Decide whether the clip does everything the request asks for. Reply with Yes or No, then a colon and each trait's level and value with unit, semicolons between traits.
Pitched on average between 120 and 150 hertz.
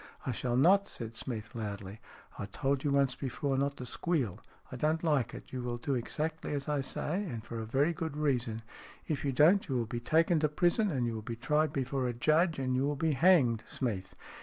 Yes: low, 135 Hz